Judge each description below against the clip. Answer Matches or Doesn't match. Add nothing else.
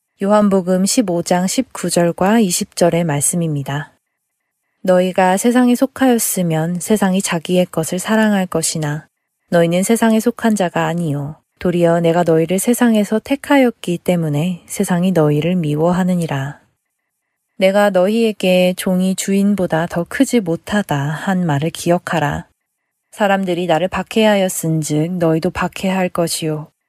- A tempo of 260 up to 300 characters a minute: Matches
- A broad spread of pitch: Doesn't match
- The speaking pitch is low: Doesn't match